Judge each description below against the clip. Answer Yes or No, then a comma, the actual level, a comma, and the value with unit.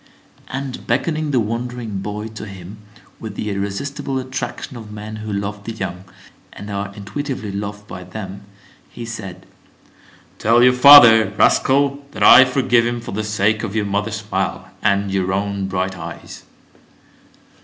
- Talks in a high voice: No, low, 105 Hz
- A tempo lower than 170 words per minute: Yes, average, 155 wpm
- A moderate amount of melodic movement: Yes, average, 3.5 semitones